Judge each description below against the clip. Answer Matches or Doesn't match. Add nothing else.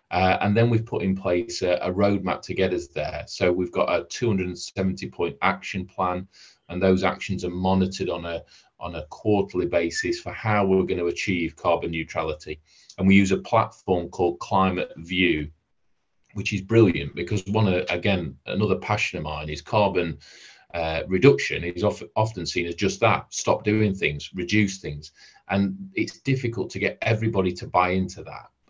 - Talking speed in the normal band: Matches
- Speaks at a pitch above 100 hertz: Doesn't match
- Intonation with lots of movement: Doesn't match